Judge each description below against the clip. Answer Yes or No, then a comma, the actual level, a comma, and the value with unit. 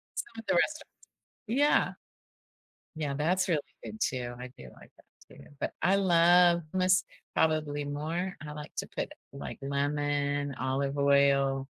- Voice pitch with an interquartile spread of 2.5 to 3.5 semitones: No, average, 4.1 semitones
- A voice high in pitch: No, medium, 150 Hz